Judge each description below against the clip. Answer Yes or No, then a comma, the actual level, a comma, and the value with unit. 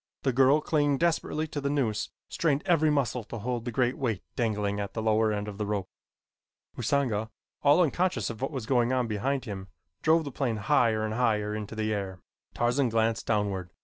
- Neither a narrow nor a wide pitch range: Yes, average, 4.6 semitones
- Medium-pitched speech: No, low, 115 Hz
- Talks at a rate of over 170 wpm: Yes, average, 195 wpm